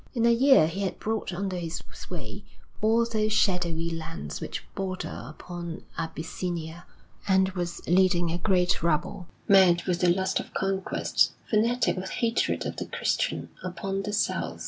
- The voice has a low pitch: No, medium, 185 Hz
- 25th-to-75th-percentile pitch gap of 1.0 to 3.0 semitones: Yes, narrow, 2.5 semitones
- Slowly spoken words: No, average, 155 wpm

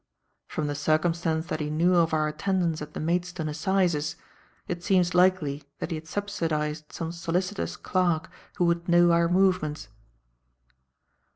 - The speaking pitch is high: No, medium, 170 Hz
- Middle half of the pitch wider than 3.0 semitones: No, narrow, 2.5 semitones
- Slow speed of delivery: No, average, 150 wpm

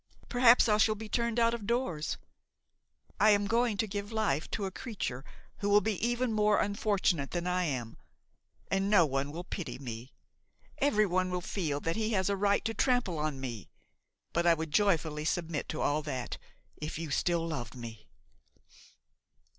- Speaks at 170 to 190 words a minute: Yes, average, 175 wpm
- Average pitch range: No, wide, 5.9 semitones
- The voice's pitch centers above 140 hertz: Yes, medium, 185 Hz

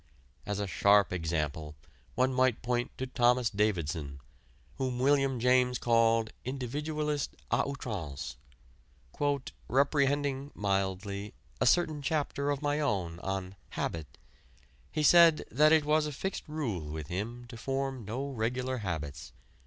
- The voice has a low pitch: Yes, low, 125 Hz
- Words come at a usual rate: No, slow, 130 wpm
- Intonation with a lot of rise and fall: Yes, wide, 6.3 semitones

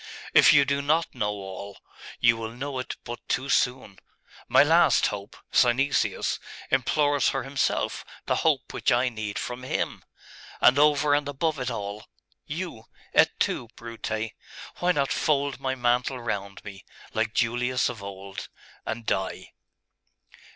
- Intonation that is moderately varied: Yes, average, 4.6 semitones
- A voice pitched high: No, low, 125 Hz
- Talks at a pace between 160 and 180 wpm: No, average, 145 wpm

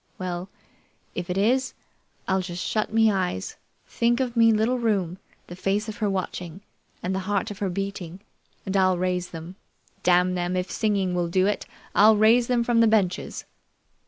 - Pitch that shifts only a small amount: No, average, 3.3 semitones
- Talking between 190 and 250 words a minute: No, average, 180 wpm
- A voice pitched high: Yes, high, 195 Hz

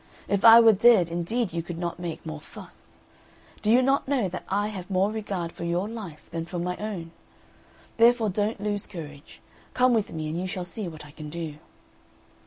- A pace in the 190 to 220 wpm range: Yes, average, 200 wpm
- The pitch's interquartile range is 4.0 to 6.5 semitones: Yes, average, 4.4 semitones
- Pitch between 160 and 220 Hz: Yes, medium, 185 Hz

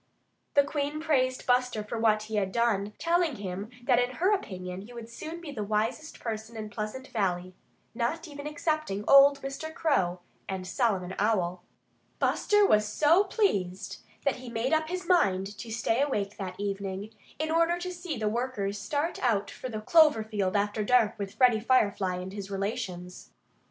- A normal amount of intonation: No, wide, 6.2 semitones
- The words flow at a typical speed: Yes, average, 175 wpm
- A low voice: No, high, 225 Hz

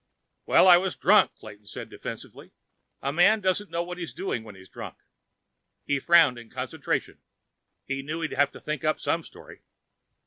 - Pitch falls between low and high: Yes, medium, 160 Hz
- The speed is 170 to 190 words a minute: Yes, average, 175 wpm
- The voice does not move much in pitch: No, average, 4.7 semitones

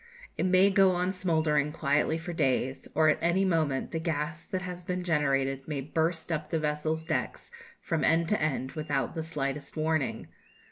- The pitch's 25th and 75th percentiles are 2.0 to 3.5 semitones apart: Yes, average, 2.8 semitones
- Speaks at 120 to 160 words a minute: No, average, 180 wpm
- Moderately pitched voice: Yes, medium, 160 Hz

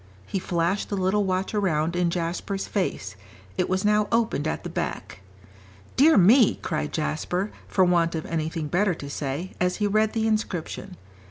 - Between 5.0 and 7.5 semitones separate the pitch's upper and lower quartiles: No, average, 3.8 semitones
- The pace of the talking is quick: No, average, 170 wpm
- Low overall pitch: No, medium, 185 Hz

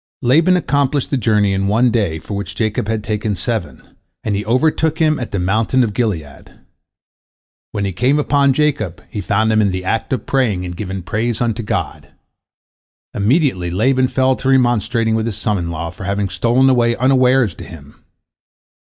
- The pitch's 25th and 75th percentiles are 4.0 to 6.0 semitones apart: Yes, average, 4.6 semitones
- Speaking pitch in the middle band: No, low, 110 Hz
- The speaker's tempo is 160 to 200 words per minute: Yes, average, 180 wpm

